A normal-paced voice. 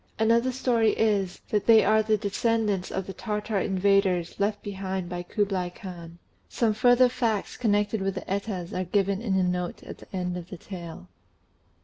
Yes: average, 175 wpm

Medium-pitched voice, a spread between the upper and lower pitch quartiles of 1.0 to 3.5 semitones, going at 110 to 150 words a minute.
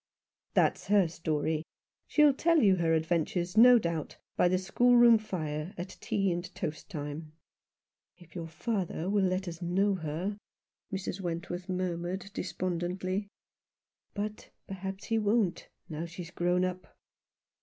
Yes: medium, 180 Hz; average, 2.8 semitones; average, 140 wpm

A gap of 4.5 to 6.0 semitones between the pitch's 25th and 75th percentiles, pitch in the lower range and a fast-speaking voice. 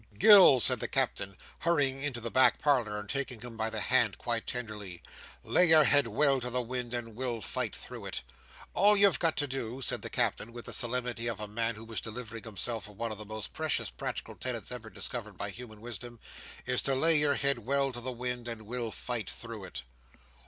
No: average, 2.9 semitones; low, 120 Hz; fast, 215 wpm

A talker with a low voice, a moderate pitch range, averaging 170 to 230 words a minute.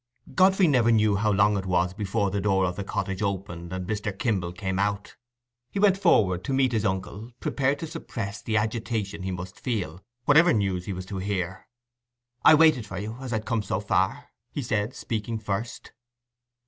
Yes: low, 105 Hz; average, 3.5 semitones; average, 190 wpm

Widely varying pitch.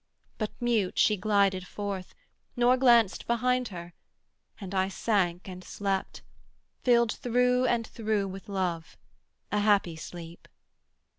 No: average, 4.1 semitones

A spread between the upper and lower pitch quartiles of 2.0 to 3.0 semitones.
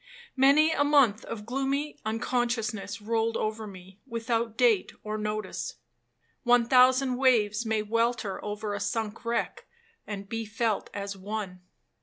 Yes: average, 2.7 semitones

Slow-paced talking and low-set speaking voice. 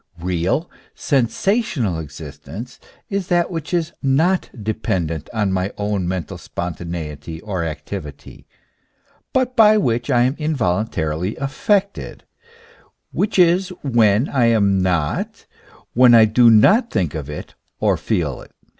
Yes: slow, 125 wpm; low, 110 Hz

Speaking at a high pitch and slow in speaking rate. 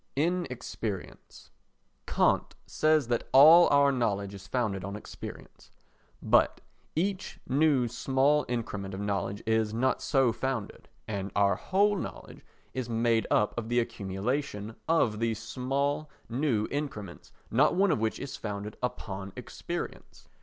No: low, 120 Hz; slow, 130 wpm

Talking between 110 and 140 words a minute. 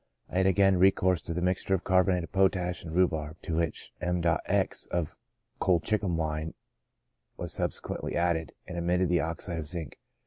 No: average, 165 wpm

